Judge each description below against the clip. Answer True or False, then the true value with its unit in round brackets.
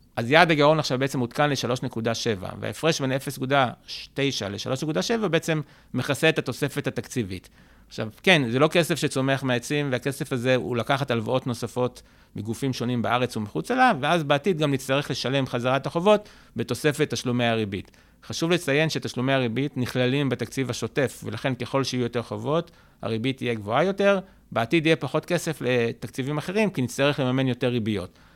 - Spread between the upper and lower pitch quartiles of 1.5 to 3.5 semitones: False (3.9 semitones)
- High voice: False (130 Hz)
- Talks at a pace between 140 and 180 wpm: True (150 wpm)